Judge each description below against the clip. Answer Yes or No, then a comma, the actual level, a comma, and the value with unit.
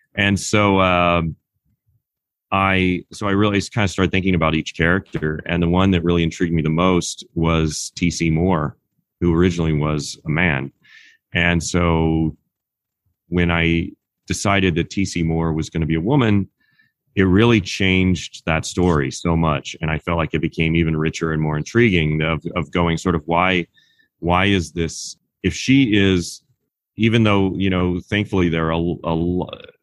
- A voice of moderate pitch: No, very low, 85 Hz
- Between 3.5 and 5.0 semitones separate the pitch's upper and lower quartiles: No, average, 2.8 semitones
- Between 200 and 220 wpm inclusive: No, average, 170 wpm